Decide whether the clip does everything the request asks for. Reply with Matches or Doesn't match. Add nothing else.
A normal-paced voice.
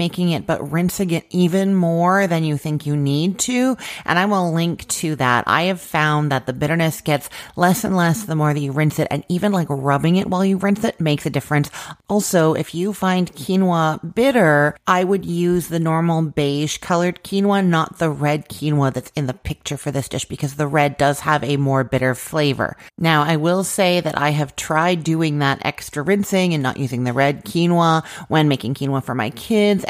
Doesn't match